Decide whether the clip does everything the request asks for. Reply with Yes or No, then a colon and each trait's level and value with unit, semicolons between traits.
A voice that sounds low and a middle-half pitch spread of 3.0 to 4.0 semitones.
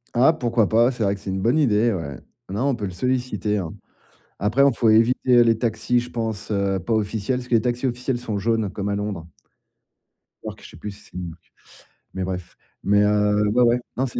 Yes: low, 110 Hz; average, 3.4 semitones